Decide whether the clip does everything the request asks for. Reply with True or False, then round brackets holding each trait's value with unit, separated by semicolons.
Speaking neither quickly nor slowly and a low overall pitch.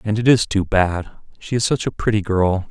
False (245 wpm; 105 Hz)